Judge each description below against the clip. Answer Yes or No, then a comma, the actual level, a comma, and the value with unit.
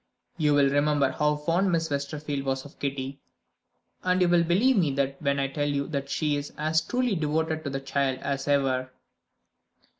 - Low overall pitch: No, medium, 145 Hz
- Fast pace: No, average, 180 wpm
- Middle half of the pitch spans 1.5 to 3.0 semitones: Yes, narrow, 2.5 semitones